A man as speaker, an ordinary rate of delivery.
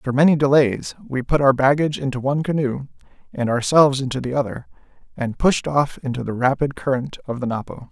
Yes: male; average, 190 wpm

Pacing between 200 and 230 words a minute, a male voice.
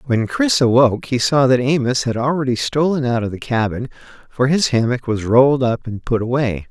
Yes: fast, 205 wpm; male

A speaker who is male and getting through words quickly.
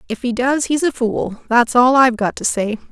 No: female; fast, 245 wpm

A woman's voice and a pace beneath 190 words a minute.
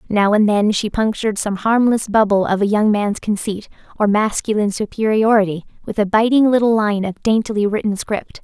Yes: female; average, 180 wpm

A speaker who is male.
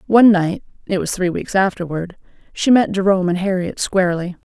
No: female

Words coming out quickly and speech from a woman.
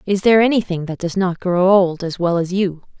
Yes: fast, 240 wpm; female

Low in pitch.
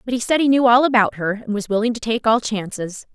No: high, 225 Hz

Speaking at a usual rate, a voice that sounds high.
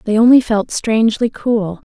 Yes: average, 155 wpm; high, 225 Hz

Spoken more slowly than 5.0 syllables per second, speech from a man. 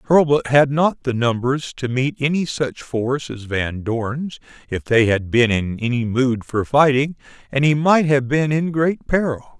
Yes: 4.2 syllables/s; male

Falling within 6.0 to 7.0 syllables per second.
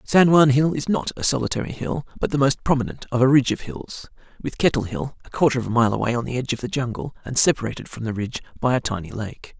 Yes: 6.7 syllables/s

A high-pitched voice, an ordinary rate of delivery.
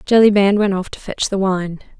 No: high, 195 Hz; fast, 210 wpm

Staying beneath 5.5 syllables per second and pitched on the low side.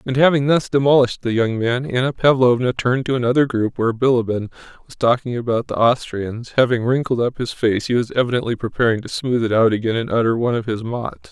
No: 6.1 syllables/s; low, 120 Hz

